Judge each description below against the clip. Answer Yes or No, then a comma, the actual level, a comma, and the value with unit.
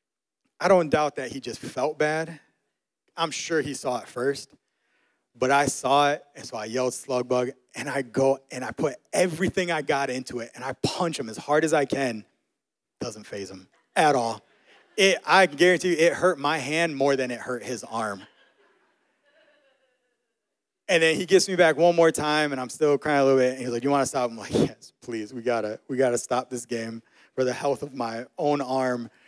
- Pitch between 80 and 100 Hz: No, medium, 140 Hz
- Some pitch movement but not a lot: Yes, average, 4.7 semitones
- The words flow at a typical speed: No, fast, 215 wpm